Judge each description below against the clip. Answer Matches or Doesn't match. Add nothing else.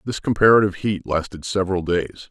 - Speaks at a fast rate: Doesn't match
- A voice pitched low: Matches